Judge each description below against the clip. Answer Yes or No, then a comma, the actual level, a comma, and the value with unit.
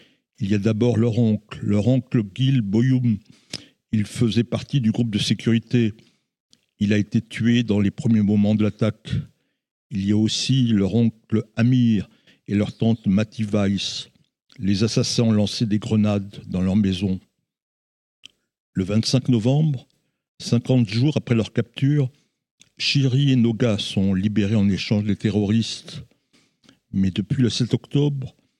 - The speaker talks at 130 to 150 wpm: Yes, slow, 145 wpm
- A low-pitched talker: Yes, low, 115 Hz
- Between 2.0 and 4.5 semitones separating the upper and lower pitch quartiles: Yes, average, 2.9 semitones